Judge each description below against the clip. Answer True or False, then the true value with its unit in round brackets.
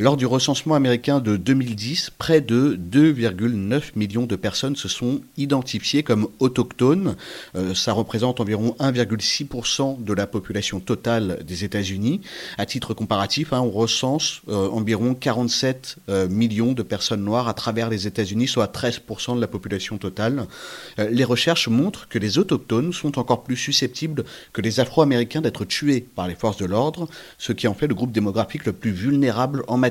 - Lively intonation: False (3.8 semitones)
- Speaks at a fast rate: False (170 wpm)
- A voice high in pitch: False (120 Hz)